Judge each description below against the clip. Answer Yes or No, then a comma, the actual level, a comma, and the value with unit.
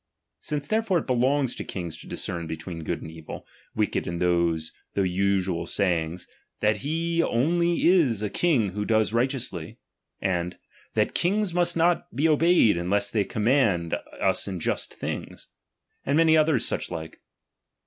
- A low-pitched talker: Yes, low, 110 Hz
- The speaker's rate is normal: Yes, average, 170 wpm